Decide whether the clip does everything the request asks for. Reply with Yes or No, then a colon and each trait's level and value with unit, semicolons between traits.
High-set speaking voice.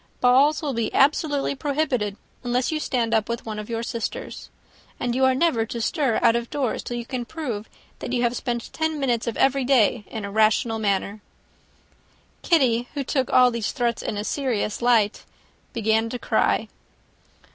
Yes: high, 240 Hz